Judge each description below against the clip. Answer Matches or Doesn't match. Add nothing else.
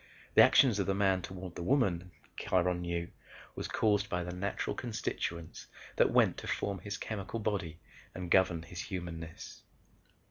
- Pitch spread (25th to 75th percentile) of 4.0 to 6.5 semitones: Doesn't match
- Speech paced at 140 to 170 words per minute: Matches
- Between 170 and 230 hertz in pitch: Doesn't match